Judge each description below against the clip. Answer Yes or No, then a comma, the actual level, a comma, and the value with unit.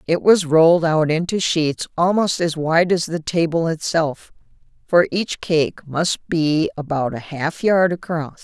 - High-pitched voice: No, medium, 165 Hz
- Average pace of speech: Yes, average, 165 wpm